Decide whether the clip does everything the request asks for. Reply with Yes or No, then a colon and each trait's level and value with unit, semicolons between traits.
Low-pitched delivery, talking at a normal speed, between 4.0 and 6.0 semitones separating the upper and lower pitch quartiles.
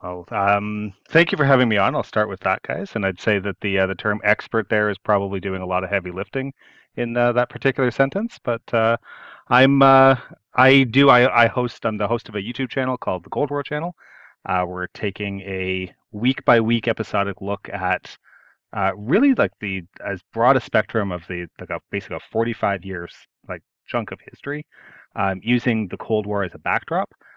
No: low, 110 Hz; fast, 210 wpm; average, 4.3 semitones